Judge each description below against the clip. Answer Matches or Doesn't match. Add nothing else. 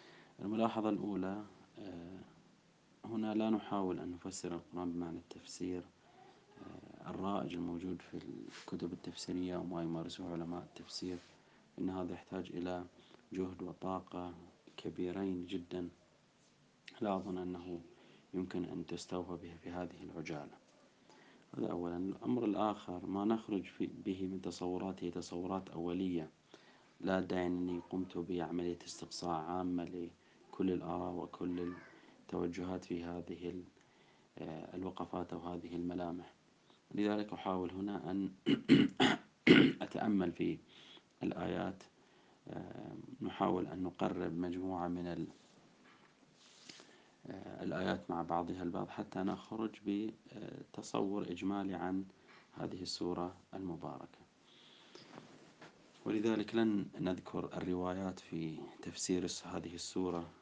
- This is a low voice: Matches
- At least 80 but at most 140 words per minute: Matches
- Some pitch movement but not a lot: Doesn't match